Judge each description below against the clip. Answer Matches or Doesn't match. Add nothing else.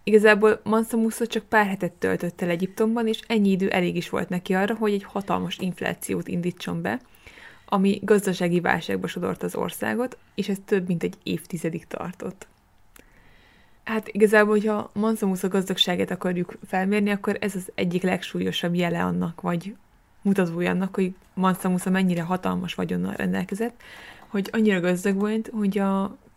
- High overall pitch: Matches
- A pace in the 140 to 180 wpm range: Matches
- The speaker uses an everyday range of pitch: Matches